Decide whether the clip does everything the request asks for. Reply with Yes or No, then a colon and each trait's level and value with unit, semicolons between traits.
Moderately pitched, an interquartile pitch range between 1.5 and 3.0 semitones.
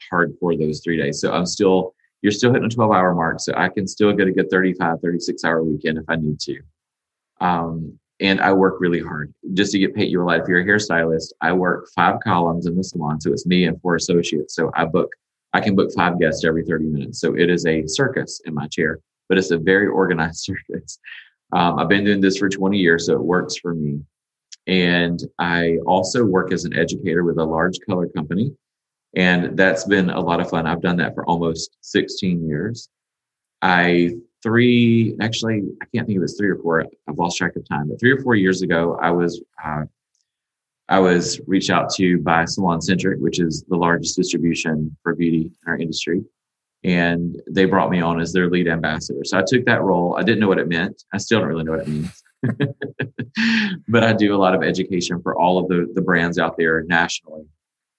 No: very low, 90 Hz; narrow, 2.5 semitones